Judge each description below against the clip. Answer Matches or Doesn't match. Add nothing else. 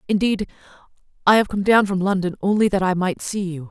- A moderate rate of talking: Doesn't match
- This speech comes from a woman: Matches